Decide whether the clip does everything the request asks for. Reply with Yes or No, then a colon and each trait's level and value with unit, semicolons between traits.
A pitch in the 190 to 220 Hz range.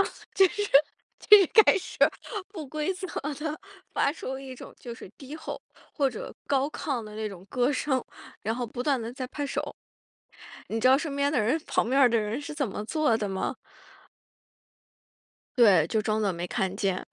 No: very high, 260 Hz